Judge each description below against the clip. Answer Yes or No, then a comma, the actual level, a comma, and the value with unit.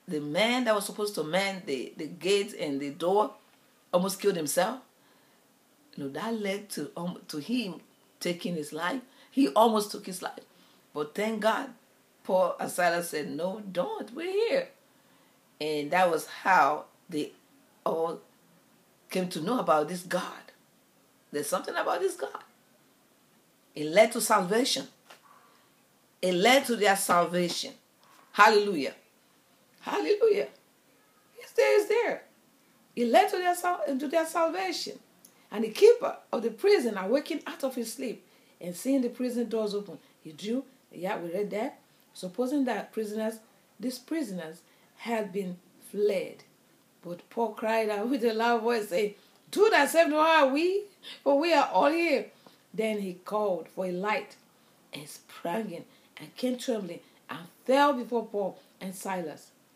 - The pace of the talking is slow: No, average, 150 wpm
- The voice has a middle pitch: No, high, 220 Hz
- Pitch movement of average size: No, wide, 6.7 semitones